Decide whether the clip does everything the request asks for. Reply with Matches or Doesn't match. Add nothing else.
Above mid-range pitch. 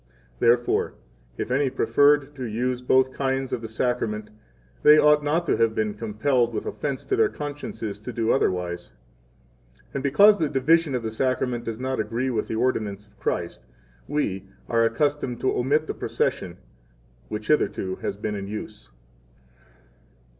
Doesn't match